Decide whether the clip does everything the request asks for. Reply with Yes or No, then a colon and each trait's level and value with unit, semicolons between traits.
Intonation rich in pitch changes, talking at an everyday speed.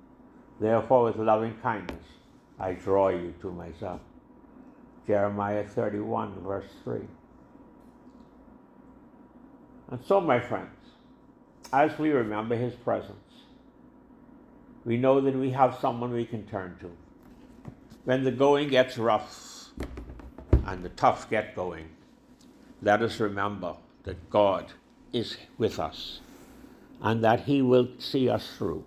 No: wide, 7.0 semitones; slow, 120 wpm